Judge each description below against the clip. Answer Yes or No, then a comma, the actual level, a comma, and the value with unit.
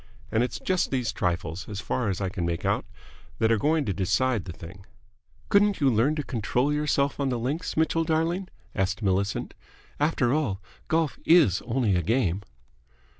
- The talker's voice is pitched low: Yes, low, 120 Hz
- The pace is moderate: Yes, average, 175 wpm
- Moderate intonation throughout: No, wide, 7.4 semitones